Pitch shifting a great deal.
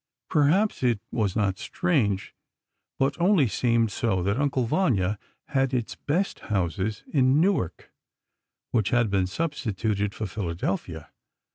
Yes: wide, 5.9 semitones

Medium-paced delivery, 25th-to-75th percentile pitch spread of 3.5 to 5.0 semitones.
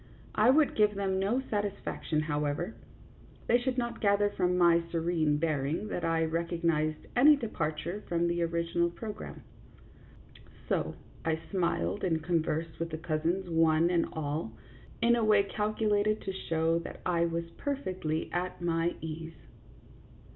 Yes: average, 145 wpm; average, 4.0 semitones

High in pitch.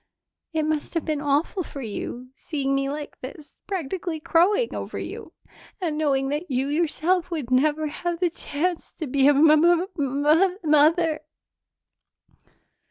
Yes: very high, 310 Hz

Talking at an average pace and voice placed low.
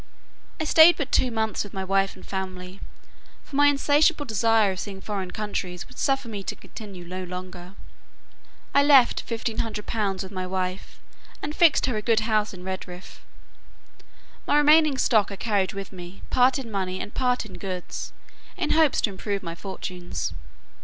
No: average, 180 wpm; high, 205 Hz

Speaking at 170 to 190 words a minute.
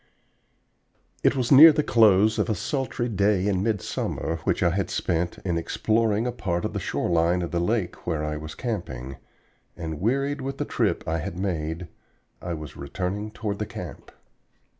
Yes: average, 180 wpm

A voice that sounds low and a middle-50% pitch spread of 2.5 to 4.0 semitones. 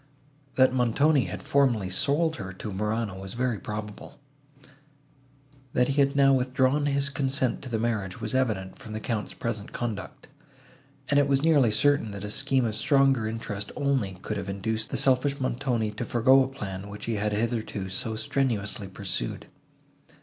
No: low, 115 Hz; average, 4.4 semitones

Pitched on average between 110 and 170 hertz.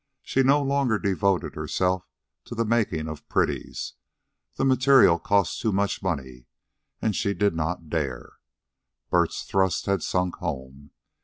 No: very low, 95 Hz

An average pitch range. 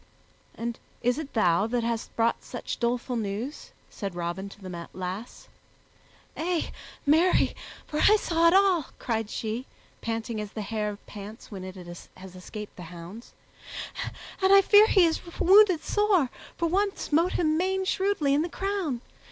No: wide, 9.0 semitones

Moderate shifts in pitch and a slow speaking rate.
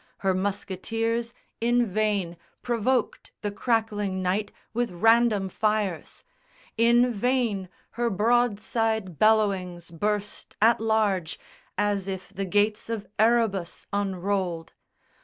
Yes: average, 3.1 semitones; slow, 100 wpm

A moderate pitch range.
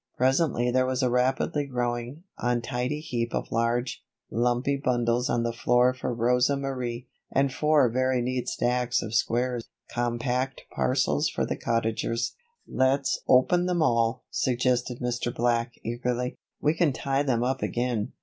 No: narrow, 1.7 semitones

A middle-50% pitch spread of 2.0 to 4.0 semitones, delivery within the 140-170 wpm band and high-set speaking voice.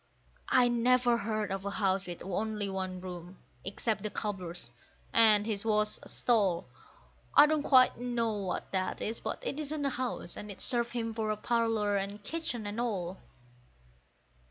Yes: average, 3.5 semitones; average, 165 wpm; high, 215 Hz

